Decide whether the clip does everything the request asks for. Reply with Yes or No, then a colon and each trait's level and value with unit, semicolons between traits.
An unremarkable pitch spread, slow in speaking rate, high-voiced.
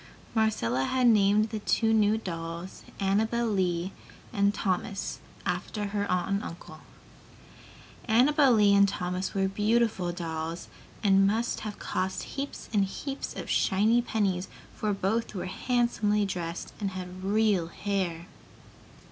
Yes: average, 3.1 semitones; slow, 130 wpm; high, 200 Hz